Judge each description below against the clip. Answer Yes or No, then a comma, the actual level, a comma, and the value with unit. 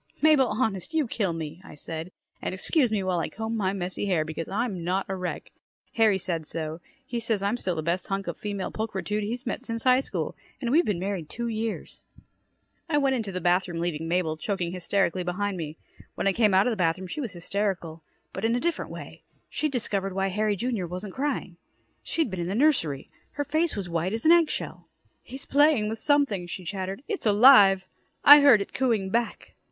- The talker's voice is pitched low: No, high, 200 Hz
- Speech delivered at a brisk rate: Yes, fast, 210 wpm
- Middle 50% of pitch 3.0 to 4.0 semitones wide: No, average, 4.9 semitones